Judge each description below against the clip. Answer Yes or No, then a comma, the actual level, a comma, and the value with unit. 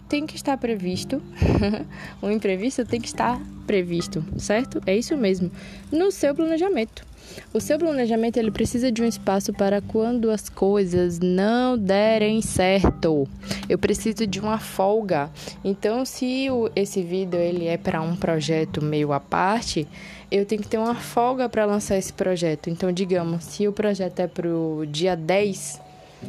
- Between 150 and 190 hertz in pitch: No, high, 200 Hz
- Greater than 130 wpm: Yes, average, 160 wpm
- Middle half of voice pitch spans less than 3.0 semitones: No, average, 3.9 semitones